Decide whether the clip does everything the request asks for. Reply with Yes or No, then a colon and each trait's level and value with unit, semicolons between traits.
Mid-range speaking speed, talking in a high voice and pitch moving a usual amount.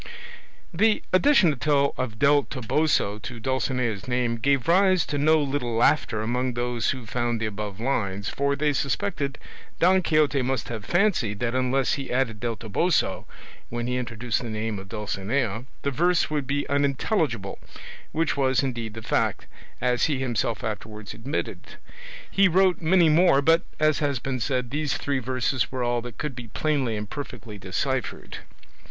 No: average, 160 wpm; low, 130 Hz; average, 4.2 semitones